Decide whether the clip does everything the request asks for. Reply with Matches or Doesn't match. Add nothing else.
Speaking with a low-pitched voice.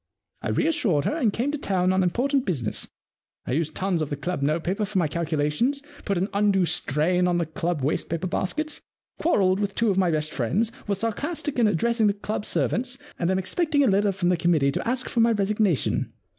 Doesn't match